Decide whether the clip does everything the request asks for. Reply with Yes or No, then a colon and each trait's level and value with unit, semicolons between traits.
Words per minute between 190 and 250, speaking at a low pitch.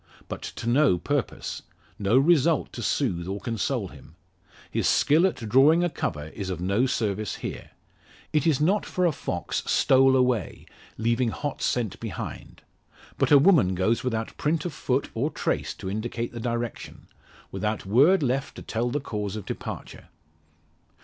No: average, 165 wpm; low, 120 Hz